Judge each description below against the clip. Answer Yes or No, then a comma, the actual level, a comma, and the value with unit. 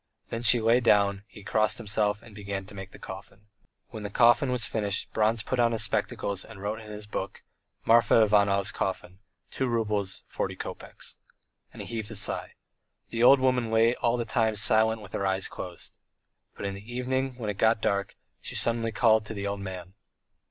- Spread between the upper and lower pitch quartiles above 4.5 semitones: No, narrow, 2.5 semitones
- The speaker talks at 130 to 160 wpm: No, average, 195 wpm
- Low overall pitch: Yes, low, 110 Hz